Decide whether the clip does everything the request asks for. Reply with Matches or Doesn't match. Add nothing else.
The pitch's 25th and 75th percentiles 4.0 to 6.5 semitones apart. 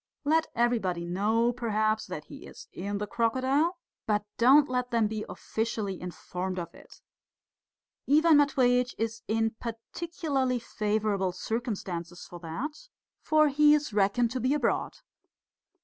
Matches